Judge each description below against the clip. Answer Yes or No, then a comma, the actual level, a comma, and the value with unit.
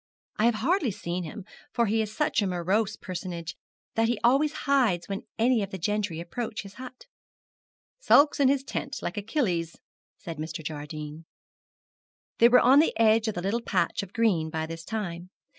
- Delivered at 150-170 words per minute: No, average, 180 wpm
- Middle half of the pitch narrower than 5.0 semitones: No, wide, 5.6 semitones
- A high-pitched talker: Yes, high, 210 Hz